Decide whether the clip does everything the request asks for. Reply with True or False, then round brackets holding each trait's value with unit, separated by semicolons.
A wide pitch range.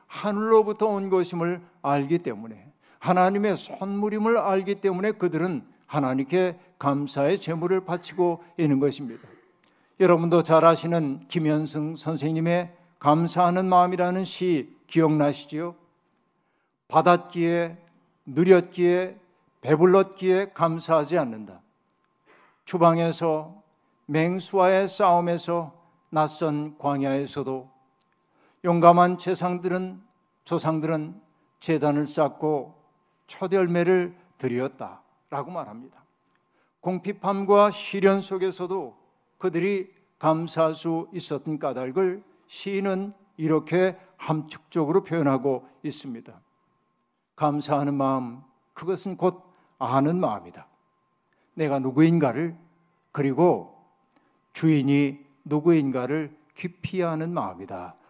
False (3.2 semitones)